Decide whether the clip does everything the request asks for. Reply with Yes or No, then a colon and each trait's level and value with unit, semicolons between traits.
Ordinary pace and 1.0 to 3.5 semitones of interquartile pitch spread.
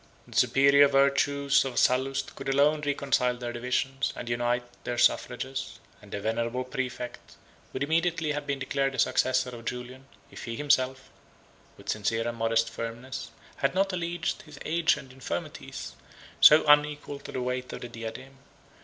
Yes: average, 160 wpm; average, 2.7 semitones